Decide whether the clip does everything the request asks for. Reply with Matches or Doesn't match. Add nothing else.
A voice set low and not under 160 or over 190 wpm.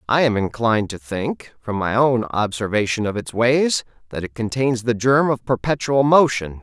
Matches